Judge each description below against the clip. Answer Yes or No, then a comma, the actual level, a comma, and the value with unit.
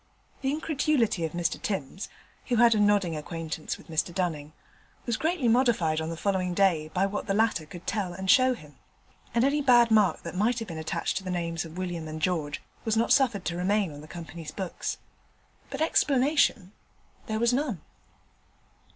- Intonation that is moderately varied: No, wide, 6.0 semitones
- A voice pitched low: No, high, 190 Hz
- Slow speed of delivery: No, average, 185 wpm